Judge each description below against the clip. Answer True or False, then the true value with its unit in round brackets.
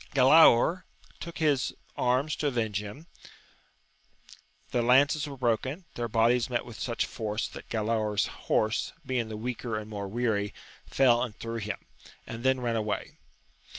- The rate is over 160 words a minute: False (150 wpm)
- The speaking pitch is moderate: False (120 Hz)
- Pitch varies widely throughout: False (3.2 semitones)